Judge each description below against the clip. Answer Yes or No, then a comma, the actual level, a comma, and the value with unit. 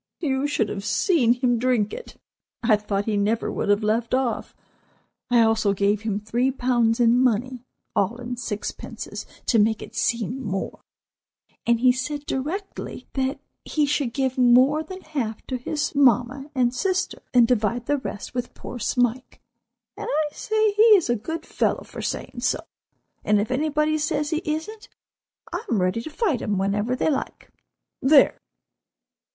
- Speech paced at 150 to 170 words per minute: Yes, average, 165 wpm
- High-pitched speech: Yes, very high, 250 Hz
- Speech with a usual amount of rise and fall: Yes, average, 4.5 semitones